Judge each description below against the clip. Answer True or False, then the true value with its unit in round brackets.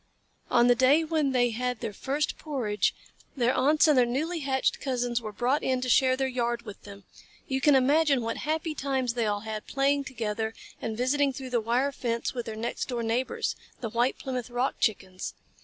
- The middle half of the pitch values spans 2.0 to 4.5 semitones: True (2.9 semitones)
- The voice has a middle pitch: False (250 Hz)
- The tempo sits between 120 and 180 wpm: False (200 wpm)